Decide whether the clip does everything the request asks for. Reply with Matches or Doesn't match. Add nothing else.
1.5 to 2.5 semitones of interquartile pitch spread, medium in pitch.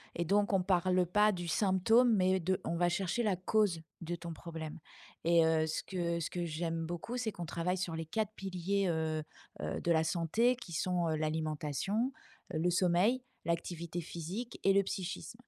Doesn't match